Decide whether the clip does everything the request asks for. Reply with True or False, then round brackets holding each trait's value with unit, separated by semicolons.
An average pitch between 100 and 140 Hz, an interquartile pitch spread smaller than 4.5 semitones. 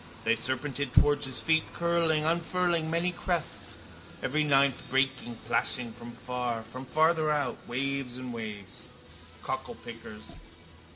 False (135 Hz; 4.8 semitones)